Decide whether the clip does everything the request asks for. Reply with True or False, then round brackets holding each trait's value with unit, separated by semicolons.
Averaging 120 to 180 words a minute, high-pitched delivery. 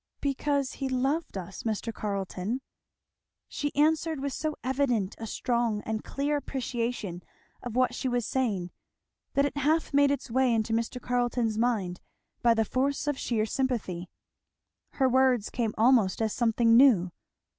True (150 wpm; 245 Hz)